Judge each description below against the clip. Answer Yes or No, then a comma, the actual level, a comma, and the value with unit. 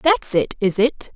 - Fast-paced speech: Yes, fast, 210 wpm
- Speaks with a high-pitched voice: Yes, high, 235 Hz